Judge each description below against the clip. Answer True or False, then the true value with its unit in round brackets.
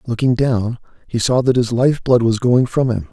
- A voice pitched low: True (120 Hz)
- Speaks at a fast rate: True (230 wpm)